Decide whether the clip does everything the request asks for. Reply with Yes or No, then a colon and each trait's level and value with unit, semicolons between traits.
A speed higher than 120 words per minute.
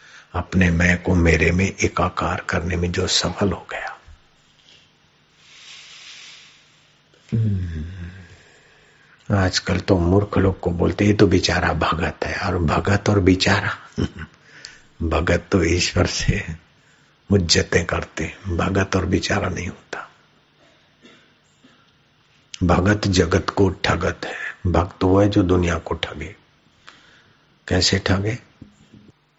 No: slow, 110 wpm